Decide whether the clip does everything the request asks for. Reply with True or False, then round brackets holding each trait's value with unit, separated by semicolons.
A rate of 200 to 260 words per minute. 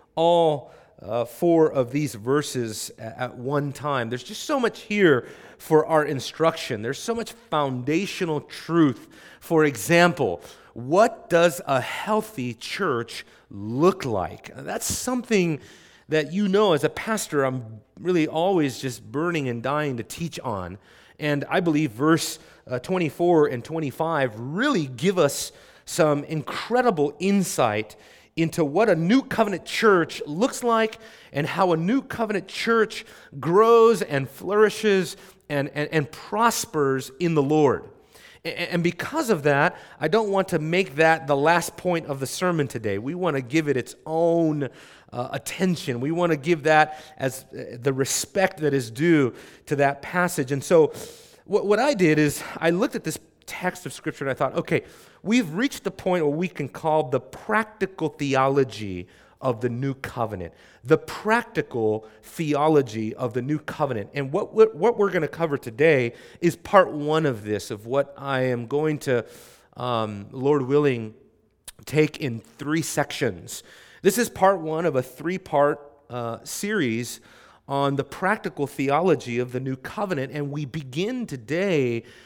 False (160 wpm)